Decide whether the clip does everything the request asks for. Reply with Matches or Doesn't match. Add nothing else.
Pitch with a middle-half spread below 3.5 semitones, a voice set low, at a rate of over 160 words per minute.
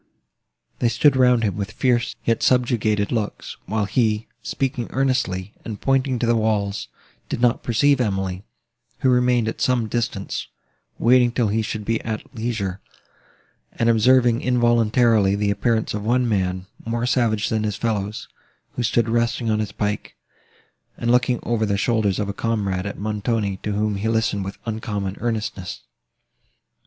Doesn't match